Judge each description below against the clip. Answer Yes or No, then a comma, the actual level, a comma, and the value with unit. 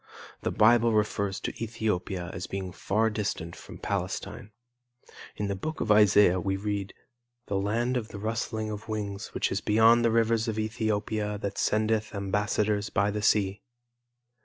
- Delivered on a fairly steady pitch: Yes, narrow, 1.7 semitones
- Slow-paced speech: No, average, 160 wpm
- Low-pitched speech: Yes, low, 105 Hz